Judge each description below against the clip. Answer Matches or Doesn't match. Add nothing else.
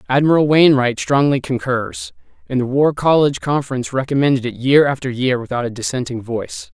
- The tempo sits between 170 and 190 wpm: Doesn't match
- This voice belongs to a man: Matches